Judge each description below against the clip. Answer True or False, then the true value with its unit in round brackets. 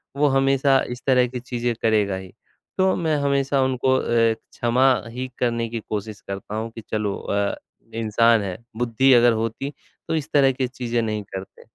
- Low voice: True (120 Hz)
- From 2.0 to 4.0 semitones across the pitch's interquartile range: True (3.3 semitones)